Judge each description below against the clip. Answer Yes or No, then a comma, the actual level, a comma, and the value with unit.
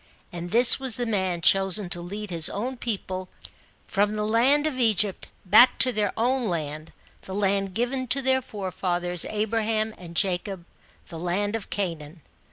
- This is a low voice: No, high, 205 Hz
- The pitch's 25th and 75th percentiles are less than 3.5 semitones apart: No, average, 4.3 semitones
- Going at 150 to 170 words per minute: Yes, average, 165 wpm